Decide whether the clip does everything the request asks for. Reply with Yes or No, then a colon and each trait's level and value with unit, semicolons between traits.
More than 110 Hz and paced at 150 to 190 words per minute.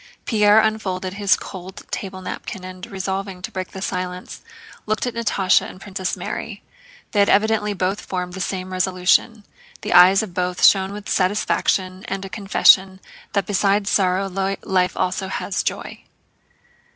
Yes: high, 190 Hz; average, 155 wpm